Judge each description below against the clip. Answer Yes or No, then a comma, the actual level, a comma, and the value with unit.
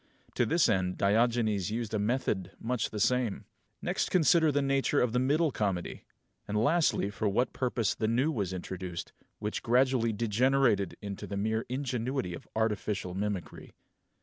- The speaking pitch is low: Yes, low, 110 Hz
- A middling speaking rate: Yes, average, 155 wpm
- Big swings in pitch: No, average, 4.2 semitones